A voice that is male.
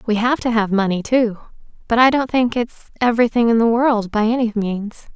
No: female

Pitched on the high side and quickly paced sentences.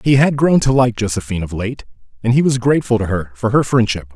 No: low, 115 Hz; fast, 245 wpm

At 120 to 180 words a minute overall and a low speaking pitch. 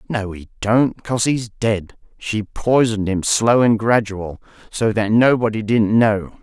Yes: average, 160 wpm; low, 110 Hz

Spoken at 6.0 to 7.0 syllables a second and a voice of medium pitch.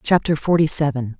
No: 5.5 syllables/s; medium, 145 Hz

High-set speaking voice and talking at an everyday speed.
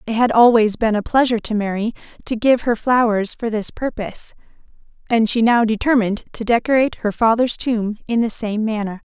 Yes: high, 225 Hz; average, 185 wpm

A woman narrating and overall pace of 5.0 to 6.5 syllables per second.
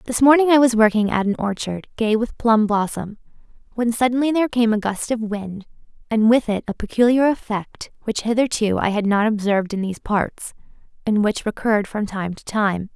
Yes: female; 5.3 syllables/s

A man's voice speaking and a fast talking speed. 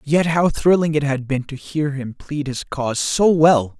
Yes: male; fast, 220 wpm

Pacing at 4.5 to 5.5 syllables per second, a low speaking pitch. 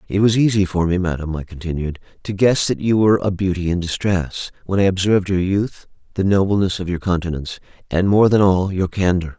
No: 5.8 syllables/s; very low, 95 Hz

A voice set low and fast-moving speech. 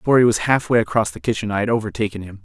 Yes: low, 110 Hz; fast, 270 wpm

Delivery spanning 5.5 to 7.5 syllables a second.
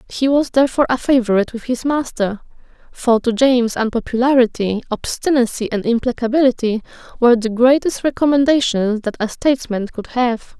Yes: 5.7 syllables/s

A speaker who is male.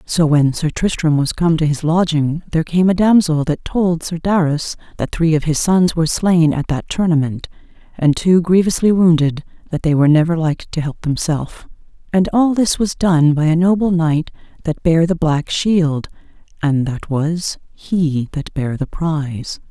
No: female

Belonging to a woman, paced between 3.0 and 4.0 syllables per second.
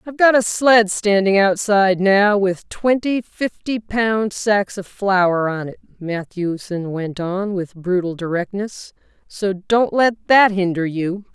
Yes: female; 3.8 syllables/s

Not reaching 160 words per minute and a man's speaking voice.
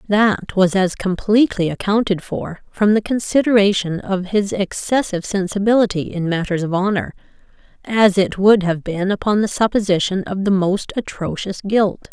No: average, 150 wpm; female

